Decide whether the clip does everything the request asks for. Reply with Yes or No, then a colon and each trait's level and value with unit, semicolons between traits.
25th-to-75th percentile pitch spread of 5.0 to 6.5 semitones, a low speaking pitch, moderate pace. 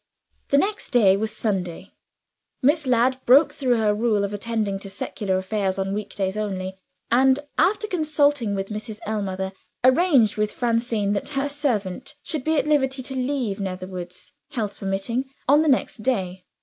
No: average, 5.3 semitones; high, 220 Hz; average, 160 wpm